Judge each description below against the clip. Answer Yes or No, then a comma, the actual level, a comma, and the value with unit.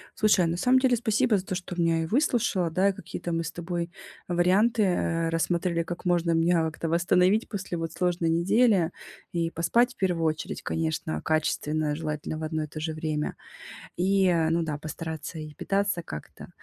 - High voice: No, medium, 170 Hz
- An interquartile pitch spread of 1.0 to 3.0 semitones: Yes, narrow, 2.6 semitones